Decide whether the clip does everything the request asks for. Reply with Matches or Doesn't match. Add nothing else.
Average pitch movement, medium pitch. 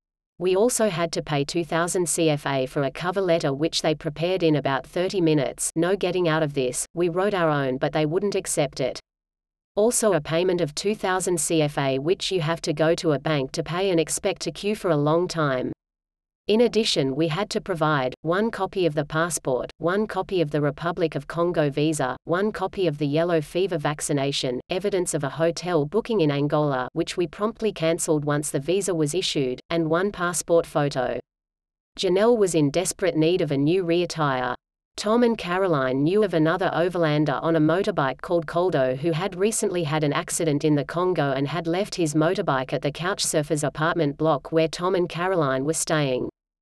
Matches